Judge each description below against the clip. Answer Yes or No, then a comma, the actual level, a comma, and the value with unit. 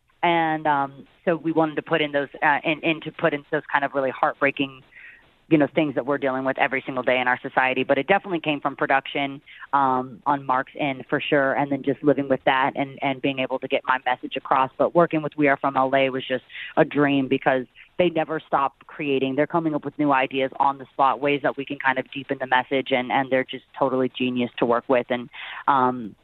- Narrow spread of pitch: Yes, narrow, 2.1 semitones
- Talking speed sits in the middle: No, fast, 240 wpm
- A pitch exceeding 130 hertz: Yes, medium, 140 Hz